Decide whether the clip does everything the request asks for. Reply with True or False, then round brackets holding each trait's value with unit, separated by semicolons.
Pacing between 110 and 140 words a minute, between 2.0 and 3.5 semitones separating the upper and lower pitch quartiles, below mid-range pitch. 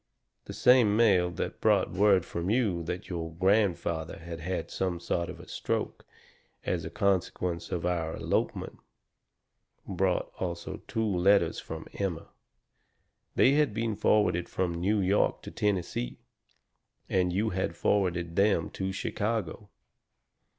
True (135 wpm; 3.1 semitones; 95 Hz)